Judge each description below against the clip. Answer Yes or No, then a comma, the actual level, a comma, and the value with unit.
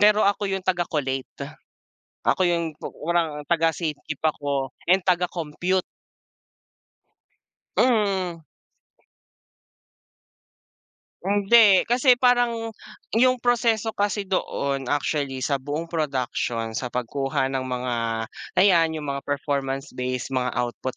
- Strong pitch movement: Yes, wide, 6.5 semitones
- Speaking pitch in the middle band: Yes, medium, 160 Hz